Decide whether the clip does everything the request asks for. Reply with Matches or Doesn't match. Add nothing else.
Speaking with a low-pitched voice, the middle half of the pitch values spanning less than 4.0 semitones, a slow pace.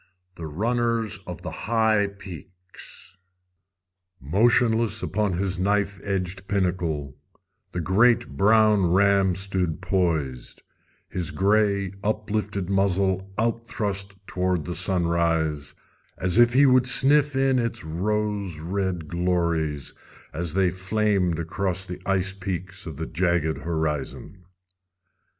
Matches